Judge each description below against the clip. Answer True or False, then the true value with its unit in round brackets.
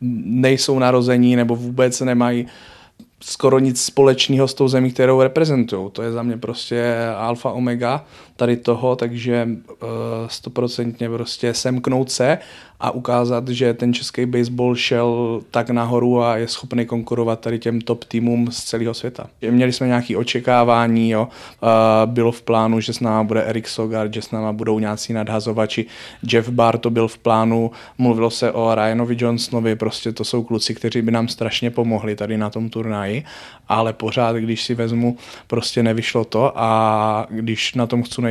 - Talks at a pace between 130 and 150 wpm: False (170 wpm)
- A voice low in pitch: True (120 Hz)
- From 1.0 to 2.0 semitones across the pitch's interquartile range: True (1.3 semitones)